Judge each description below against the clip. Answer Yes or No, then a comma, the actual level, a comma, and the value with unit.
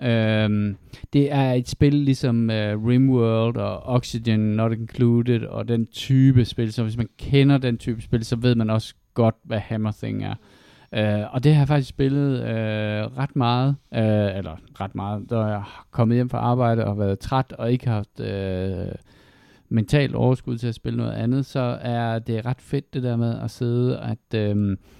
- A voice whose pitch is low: Yes, low, 115 Hz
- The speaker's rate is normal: Yes, average, 190 wpm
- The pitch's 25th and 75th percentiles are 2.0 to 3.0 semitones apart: Yes, narrow, 2.6 semitones